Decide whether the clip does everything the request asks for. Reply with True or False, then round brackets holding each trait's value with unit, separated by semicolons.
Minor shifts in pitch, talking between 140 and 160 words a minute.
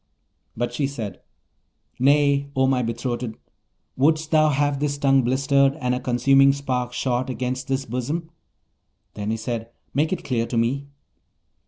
True (2.3 semitones; 145 wpm)